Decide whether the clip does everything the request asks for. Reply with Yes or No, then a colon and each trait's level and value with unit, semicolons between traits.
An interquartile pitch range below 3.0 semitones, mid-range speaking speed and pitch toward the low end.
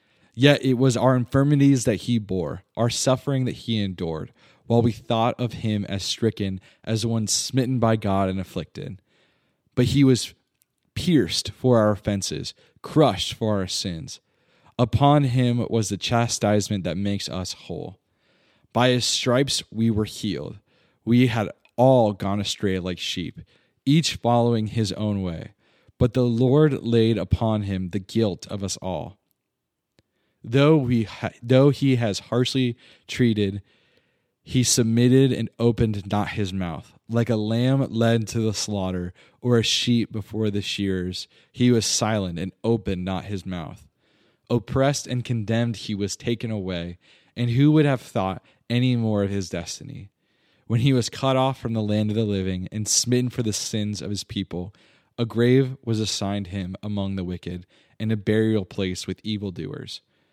No: average, 3.7 semitones; average, 160 wpm; low, 110 Hz